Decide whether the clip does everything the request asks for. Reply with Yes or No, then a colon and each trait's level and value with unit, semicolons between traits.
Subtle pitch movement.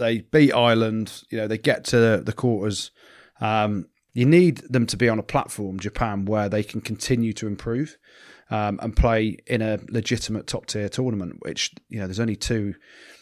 Yes: narrow, 2.2 semitones